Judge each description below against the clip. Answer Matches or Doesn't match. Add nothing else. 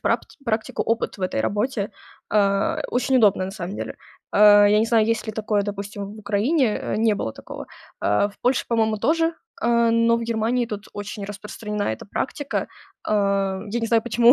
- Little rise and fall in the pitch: Matches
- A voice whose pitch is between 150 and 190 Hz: Doesn't match